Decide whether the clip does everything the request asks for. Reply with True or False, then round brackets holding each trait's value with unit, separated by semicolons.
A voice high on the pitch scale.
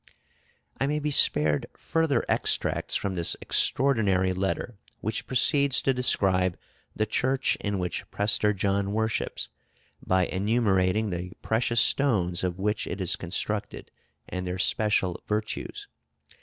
False (105 Hz)